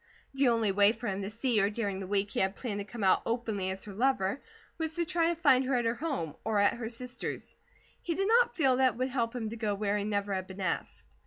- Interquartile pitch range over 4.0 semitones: Yes, average, 4.4 semitones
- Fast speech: Yes, fast, 270 wpm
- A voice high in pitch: Yes, high, 230 Hz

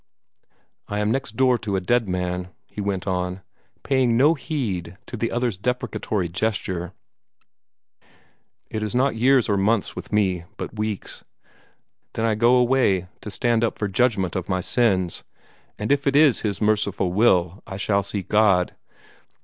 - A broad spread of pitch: No, average, 4.3 semitones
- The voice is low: Yes, low, 105 Hz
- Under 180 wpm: Yes, average, 160 wpm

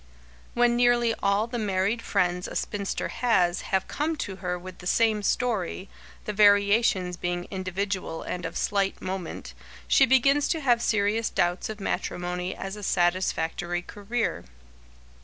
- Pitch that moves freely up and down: No, average, 4.2 semitones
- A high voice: Yes, high, 200 Hz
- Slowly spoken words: No, average, 145 wpm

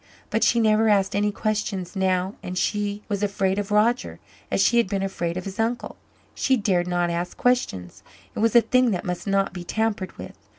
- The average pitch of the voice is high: Yes, high, 200 Hz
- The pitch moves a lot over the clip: No, average, 3.1 semitones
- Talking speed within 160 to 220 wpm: Yes, fast, 205 wpm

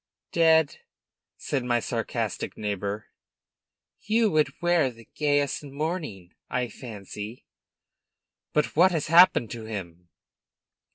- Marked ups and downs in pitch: Yes, wide, 7.1 semitones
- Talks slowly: Yes, slow, 110 wpm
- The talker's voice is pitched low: Yes, low, 130 Hz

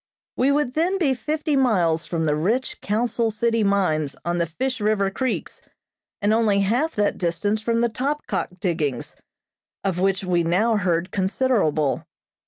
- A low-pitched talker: No, high, 205 Hz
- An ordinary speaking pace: Yes, average, 155 wpm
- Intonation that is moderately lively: No, wide, 5.8 semitones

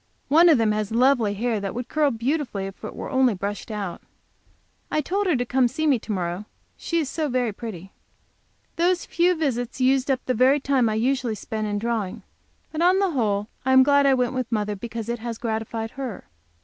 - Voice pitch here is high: Yes, high, 245 Hz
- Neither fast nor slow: No, fast, 215 wpm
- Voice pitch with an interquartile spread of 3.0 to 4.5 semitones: Yes, average, 4.2 semitones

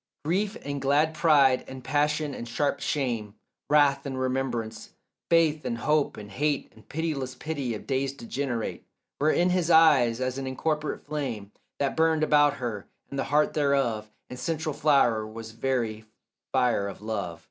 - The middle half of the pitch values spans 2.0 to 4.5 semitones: Yes, average, 4.2 semitones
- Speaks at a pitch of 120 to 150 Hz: Yes, low, 135 Hz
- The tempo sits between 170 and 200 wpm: No, average, 160 wpm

